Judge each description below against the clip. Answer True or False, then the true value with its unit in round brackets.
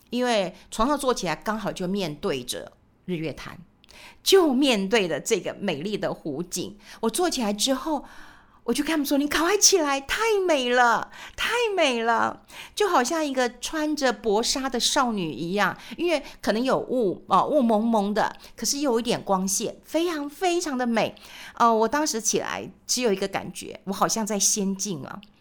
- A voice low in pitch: False (235 Hz)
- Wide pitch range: True (6.6 semitones)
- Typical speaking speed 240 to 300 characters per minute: True (255 characters per minute)